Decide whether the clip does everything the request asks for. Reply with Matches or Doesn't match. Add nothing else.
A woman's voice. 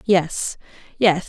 Matches